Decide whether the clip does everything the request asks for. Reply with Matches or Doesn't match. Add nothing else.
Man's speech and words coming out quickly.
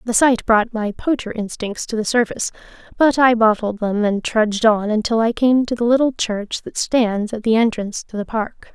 Doesn't match